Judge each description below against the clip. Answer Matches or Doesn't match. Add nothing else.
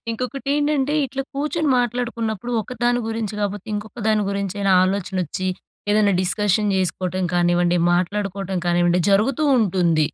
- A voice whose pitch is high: Matches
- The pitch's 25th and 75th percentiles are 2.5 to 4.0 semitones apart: Doesn't match